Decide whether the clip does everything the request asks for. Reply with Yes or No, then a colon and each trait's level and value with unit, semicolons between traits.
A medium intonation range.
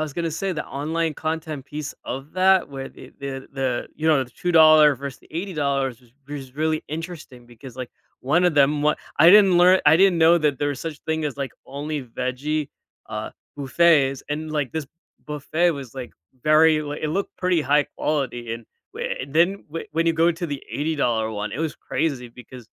Yes: average, 3.2 semitones